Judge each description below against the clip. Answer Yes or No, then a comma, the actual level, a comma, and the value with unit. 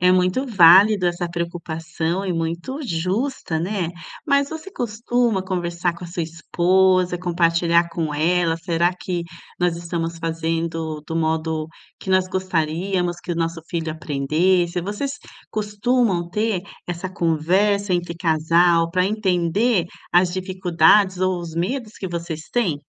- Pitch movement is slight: Yes, narrow, 2.3 semitones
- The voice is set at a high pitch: No, medium, 175 Hz